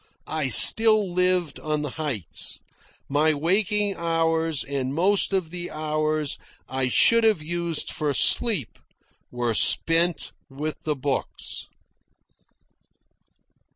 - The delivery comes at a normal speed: No, slow, 110 wpm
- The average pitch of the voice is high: No, medium, 160 Hz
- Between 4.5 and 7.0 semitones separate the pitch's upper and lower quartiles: No, average, 3.6 semitones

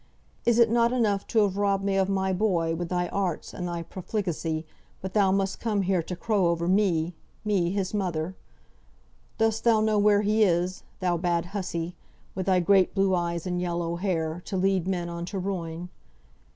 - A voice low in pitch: No, medium, 185 Hz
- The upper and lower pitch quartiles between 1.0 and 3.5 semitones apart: Yes, average, 2.7 semitones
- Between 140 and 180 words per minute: No, average, 190 wpm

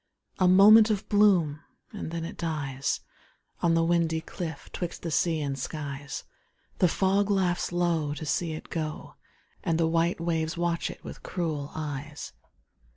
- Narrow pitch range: Yes, narrow, 2.3 semitones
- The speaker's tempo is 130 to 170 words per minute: Yes, average, 155 wpm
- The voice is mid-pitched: Yes, medium, 165 Hz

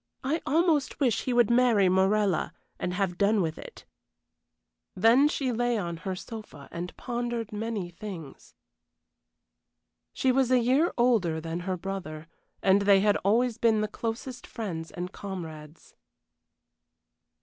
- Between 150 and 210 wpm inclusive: No, average, 140 wpm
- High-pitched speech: Yes, high, 210 Hz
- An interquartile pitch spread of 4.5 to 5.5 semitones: Yes, average, 5.1 semitones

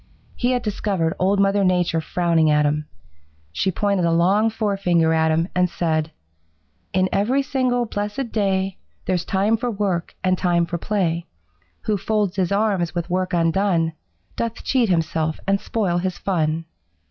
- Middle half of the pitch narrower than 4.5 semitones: Yes, average, 3.5 semitones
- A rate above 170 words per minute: No, average, 160 wpm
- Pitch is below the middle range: No, medium, 185 Hz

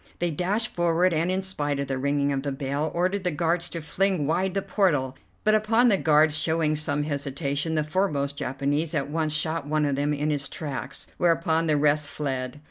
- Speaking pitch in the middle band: Yes, medium, 155 Hz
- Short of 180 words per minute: No, fast, 205 wpm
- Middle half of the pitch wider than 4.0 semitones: No, average, 3.3 semitones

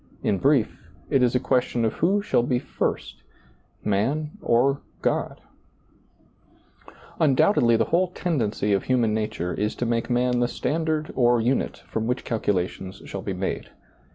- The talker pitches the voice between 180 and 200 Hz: No, low, 120 Hz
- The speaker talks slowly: No, average, 155 wpm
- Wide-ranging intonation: No, average, 4.2 semitones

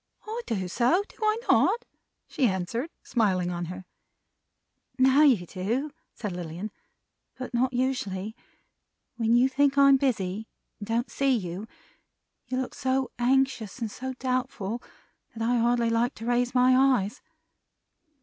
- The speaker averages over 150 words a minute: No, average, 140 wpm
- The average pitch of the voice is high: Yes, high, 240 Hz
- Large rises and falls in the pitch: No, average, 4.1 semitones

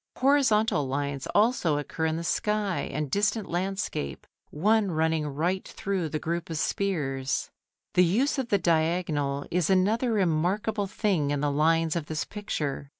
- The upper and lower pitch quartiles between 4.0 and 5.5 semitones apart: Yes, average, 5.2 semitones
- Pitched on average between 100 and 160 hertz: No, medium, 170 Hz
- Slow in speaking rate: No, average, 150 wpm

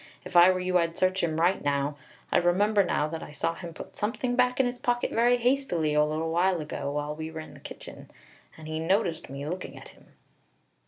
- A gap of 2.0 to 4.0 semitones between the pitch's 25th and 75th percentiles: No, average, 4.6 semitones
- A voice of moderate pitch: Yes, medium, 170 Hz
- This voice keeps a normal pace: No, fast, 225 wpm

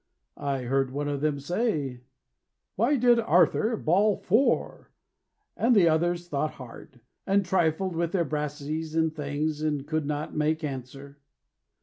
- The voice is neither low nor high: Yes, medium, 155 Hz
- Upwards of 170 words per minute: No, average, 140 wpm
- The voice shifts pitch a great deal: No, average, 3.9 semitones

